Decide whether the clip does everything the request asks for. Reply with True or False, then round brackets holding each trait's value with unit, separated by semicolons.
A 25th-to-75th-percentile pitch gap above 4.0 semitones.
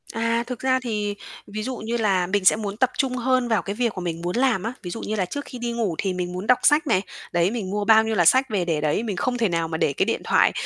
True (4.6 semitones)